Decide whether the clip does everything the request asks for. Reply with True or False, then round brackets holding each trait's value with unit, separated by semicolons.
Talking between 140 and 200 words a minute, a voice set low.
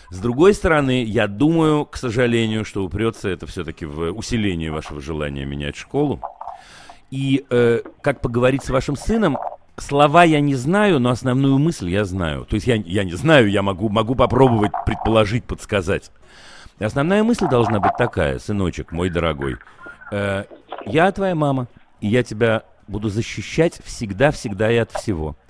True (155 wpm; 115 Hz)